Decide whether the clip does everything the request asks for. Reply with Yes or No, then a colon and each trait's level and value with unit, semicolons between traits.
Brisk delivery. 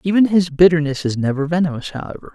No: average, 180 wpm